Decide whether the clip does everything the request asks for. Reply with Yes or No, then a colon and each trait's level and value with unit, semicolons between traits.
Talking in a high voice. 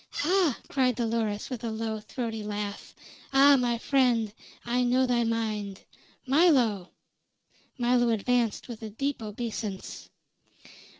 Yes: high, 235 Hz